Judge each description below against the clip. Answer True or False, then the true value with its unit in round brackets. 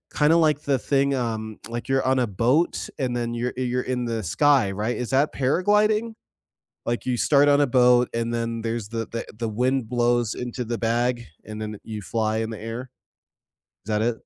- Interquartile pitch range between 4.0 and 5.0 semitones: False (2.7 semitones)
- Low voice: True (120 Hz)